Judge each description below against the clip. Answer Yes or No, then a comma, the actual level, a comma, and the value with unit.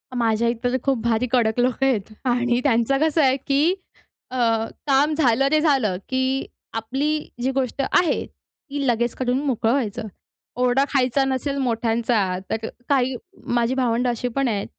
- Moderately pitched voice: No, very high, 250 Hz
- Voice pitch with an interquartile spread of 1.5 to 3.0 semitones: Yes, average, 2.7 semitones